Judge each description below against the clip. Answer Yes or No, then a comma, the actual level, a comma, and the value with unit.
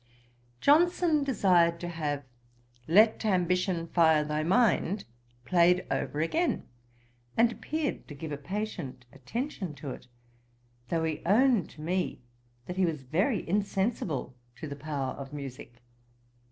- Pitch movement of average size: No, wide, 5.8 semitones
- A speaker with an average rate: No, slow, 130 wpm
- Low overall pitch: No, medium, 170 Hz